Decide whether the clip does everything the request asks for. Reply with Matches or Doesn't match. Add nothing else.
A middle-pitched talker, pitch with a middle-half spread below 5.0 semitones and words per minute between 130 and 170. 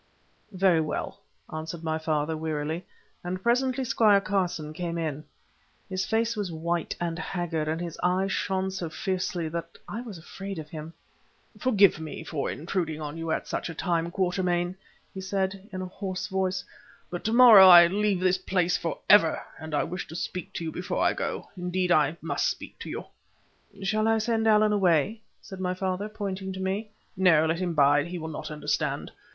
Doesn't match